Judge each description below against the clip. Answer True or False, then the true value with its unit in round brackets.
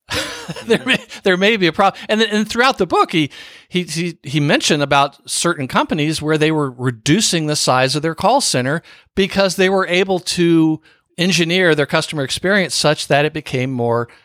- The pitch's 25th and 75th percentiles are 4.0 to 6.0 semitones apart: True (4.4 semitones)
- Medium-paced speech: True (180 wpm)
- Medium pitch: True (165 Hz)